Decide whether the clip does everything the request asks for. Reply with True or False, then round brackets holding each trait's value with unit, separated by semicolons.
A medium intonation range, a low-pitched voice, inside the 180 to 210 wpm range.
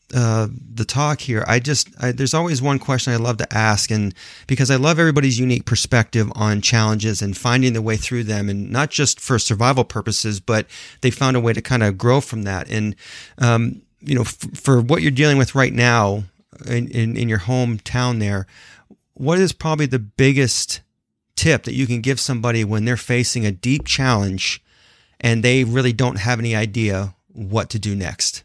True (3.3 semitones; 120 Hz; 195 wpm)